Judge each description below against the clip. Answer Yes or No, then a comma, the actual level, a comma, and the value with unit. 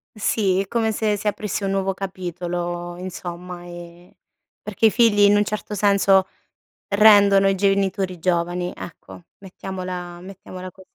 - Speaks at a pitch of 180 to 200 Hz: Yes, high, 190 Hz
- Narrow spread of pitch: Yes, narrow, 2.3 semitones